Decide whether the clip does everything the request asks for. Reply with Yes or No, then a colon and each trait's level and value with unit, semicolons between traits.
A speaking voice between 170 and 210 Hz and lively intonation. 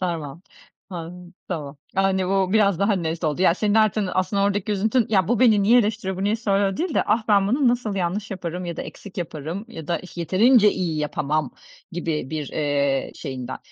No: high, 190 Hz; average, 4.0 semitones